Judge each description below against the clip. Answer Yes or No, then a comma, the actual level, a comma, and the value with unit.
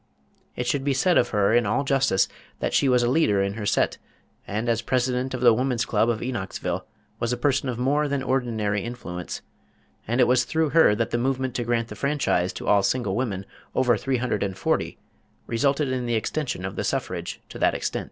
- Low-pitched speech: Yes, low, 120 Hz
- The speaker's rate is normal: No, fast, 215 wpm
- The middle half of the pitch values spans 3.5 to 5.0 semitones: No, average, 3.1 semitones